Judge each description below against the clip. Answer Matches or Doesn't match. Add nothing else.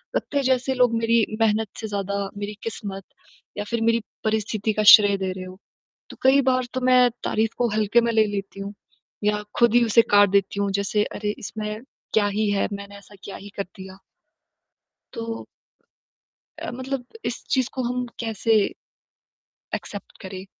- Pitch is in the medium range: Doesn't match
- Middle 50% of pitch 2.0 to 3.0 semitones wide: Matches